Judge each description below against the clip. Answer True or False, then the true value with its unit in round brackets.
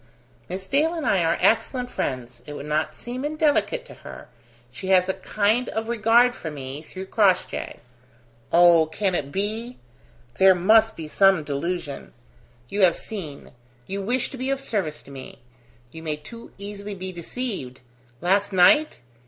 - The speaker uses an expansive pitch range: True (6.0 semitones)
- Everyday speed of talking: True (160 wpm)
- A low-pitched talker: False (190 Hz)